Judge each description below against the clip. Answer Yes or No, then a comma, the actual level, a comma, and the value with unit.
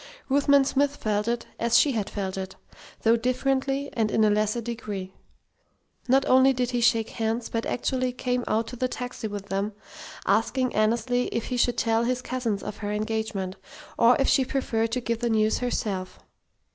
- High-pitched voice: Yes, high, 230 Hz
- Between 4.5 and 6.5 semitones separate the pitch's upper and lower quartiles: No, average, 2.9 semitones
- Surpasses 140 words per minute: Yes, average, 185 wpm